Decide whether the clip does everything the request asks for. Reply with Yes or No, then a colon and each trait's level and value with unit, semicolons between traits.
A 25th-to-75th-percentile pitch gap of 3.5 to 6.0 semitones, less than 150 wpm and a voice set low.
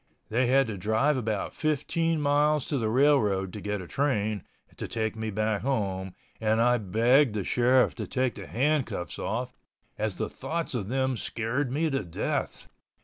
No: average, 4.3 semitones; average, 175 wpm; low, 120 Hz